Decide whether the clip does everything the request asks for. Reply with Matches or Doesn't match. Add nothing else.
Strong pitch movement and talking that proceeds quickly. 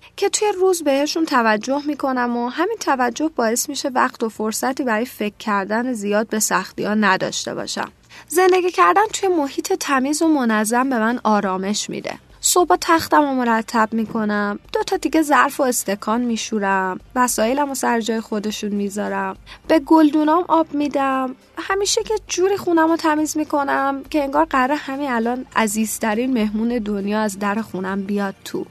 Matches